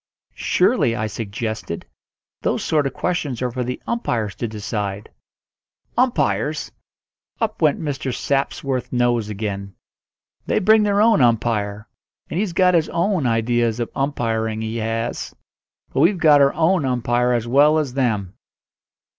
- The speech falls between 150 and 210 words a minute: No, average, 140 wpm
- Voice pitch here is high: No, low, 125 Hz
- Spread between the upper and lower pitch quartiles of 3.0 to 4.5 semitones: No, wide, 5.5 semitones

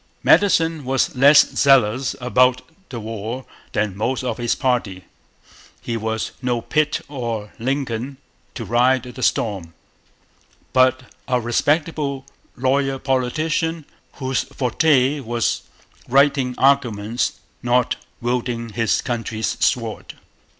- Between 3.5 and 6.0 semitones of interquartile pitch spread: No, average, 2.8 semitones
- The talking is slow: Yes, slow, 110 wpm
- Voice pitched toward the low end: Yes, low, 125 Hz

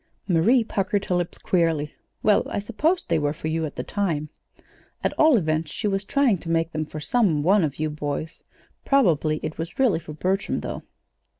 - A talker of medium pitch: Yes, medium, 170 Hz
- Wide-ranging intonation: No, average, 4.7 semitones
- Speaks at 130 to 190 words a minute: No, average, 200 wpm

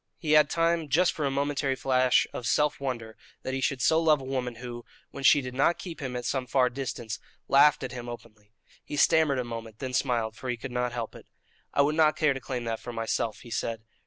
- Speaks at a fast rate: Yes, fast, 240 wpm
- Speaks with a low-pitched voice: Yes, low, 130 Hz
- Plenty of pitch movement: No, average, 3.1 semitones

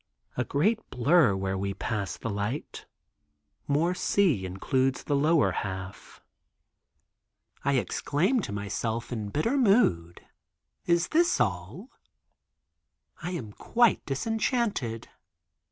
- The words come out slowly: Yes, slow, 105 wpm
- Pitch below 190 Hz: Yes, low, 135 Hz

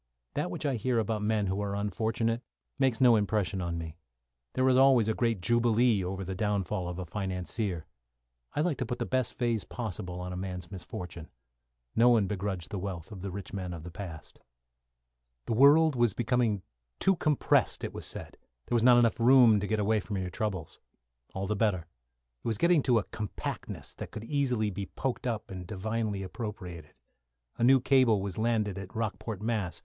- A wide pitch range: No, average, 4.0 semitones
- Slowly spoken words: No, average, 195 wpm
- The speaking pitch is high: No, low, 105 Hz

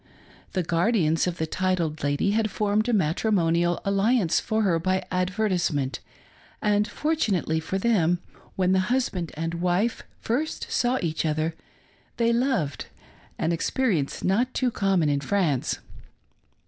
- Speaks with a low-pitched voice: No, medium, 185 Hz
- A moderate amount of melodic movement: Yes, average, 4.8 semitones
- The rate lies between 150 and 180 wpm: No, average, 140 wpm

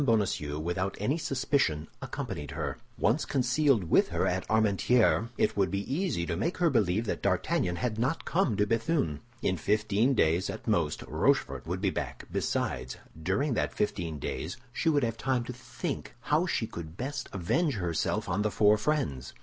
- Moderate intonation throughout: No, wide, 6.9 semitones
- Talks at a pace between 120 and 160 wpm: No, average, 175 wpm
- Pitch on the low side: Yes, low, 105 Hz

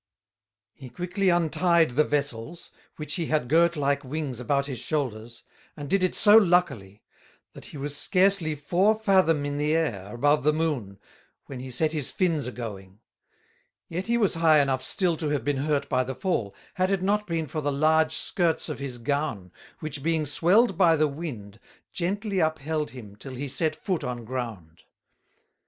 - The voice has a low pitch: No, medium, 150 Hz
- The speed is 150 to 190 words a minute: Yes, average, 180 wpm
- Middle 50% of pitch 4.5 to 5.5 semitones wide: Yes, average, 4.8 semitones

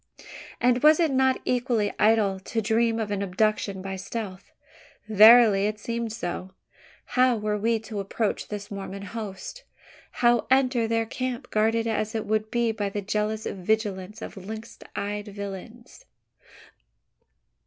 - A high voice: Yes, high, 220 Hz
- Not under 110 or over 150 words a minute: Yes, average, 145 wpm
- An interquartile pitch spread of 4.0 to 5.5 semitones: No, narrow, 2.5 semitones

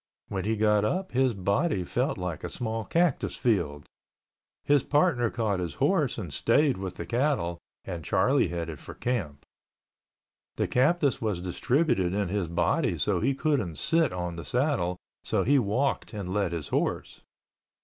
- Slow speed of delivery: No, average, 160 wpm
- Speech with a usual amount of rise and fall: No, wide, 7.2 semitones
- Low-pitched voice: Yes, low, 105 Hz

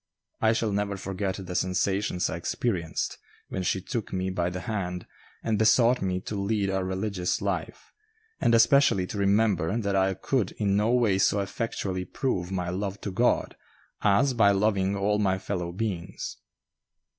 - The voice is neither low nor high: No, low, 100 Hz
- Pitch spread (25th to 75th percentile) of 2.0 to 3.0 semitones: Yes, narrow, 2.5 semitones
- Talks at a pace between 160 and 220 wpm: Yes, average, 165 wpm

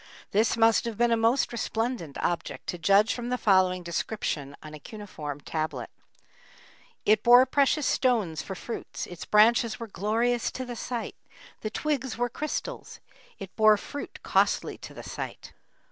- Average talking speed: Yes, average, 160 wpm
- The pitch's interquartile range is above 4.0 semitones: Yes, average, 4.6 semitones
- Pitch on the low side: No, high, 220 Hz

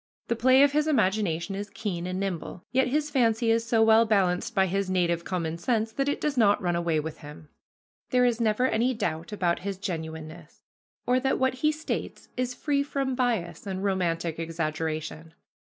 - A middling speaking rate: Yes, average, 185 wpm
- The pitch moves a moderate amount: No, wide, 6.5 semitones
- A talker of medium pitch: No, high, 200 Hz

